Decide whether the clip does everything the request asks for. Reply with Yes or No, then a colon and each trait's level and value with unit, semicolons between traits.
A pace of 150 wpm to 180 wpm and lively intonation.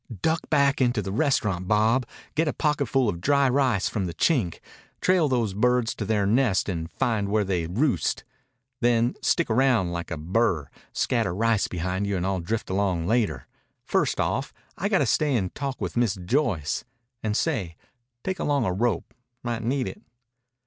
Yes: average, 175 wpm; wide, 6.0 semitones